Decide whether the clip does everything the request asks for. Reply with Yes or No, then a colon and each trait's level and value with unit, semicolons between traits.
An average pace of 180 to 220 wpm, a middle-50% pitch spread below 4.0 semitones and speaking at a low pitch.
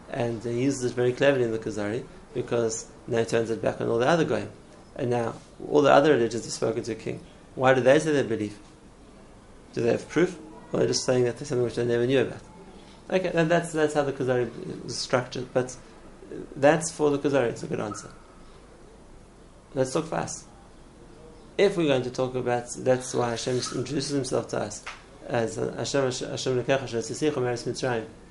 Yes: average, 200 wpm; average, 2.8 semitones; low, 125 Hz